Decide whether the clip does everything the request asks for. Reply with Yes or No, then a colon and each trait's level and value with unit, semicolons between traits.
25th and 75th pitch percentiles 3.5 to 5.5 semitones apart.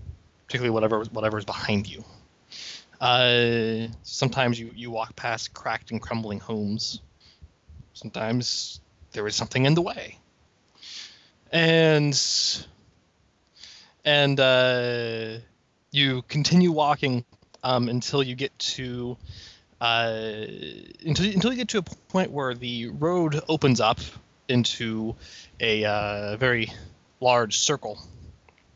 Yes: average, 3.8 semitones